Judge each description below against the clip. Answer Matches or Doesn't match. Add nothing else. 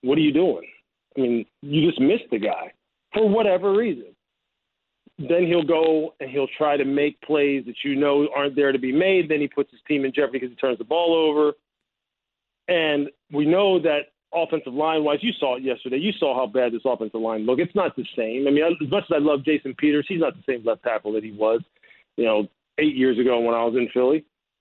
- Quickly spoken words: Matches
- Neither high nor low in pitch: Matches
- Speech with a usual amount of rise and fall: Matches